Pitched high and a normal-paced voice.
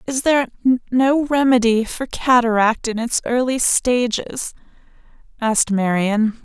No: high, 240 Hz; slow, 110 wpm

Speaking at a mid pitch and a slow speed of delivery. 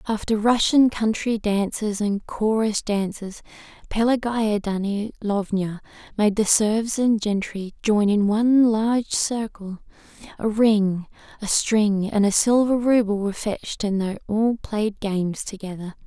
No: high, 210 Hz; slow, 130 wpm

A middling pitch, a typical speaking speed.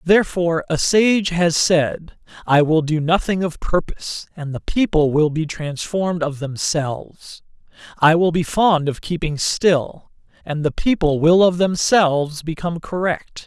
Yes: medium, 165 Hz; average, 150 wpm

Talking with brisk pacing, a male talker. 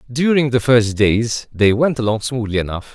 No: average, 185 wpm; male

